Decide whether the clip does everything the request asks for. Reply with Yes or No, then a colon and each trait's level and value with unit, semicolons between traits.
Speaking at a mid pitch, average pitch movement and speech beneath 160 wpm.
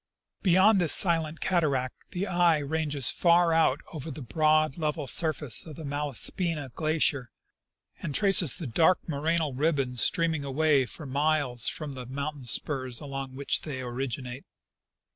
Yes: medium, 150 Hz; average, 3.4 semitones; average, 145 wpm